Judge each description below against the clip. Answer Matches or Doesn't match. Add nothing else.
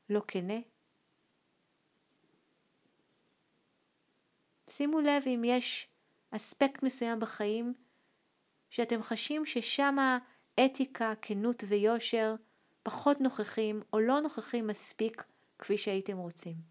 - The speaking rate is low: Matches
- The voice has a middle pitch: Doesn't match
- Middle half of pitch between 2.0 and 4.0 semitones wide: Matches